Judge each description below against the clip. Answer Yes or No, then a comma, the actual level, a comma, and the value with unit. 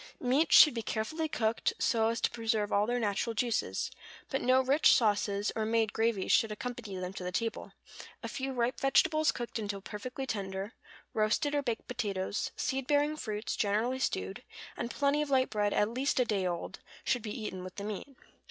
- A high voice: Yes, high, 225 Hz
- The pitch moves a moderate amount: Yes, average, 3.9 semitones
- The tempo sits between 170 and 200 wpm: Yes, average, 190 wpm